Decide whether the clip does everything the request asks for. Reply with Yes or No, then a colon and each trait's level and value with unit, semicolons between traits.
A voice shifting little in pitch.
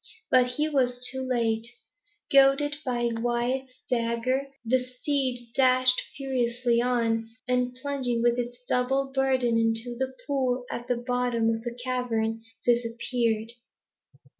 Yes: narrow, 1.6 semitones